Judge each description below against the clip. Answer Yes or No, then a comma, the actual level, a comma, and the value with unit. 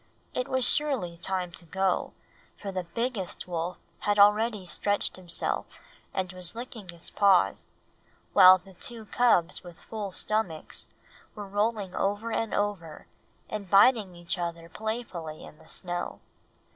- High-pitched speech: Yes, high, 195 Hz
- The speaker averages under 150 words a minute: Yes, average, 140 wpm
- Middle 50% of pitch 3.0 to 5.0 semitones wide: Yes, average, 3.6 semitones